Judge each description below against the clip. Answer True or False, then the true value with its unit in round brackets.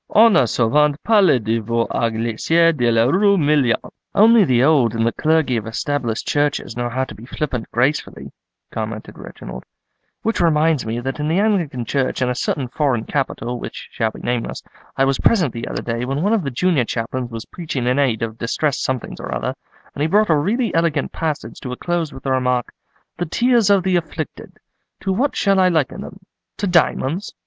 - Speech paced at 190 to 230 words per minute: True (200 wpm)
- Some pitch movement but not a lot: False (6.1 semitones)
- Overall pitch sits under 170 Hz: True (140 Hz)